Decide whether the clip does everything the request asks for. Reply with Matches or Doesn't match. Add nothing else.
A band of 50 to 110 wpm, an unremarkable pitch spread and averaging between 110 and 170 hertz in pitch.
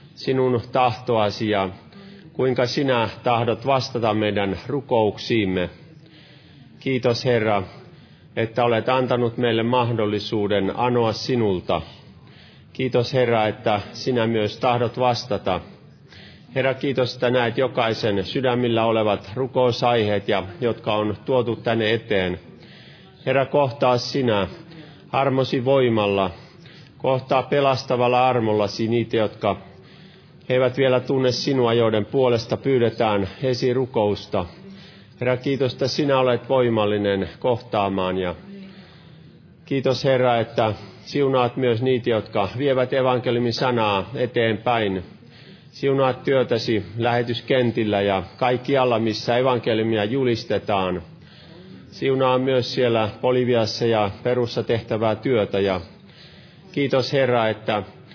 Matches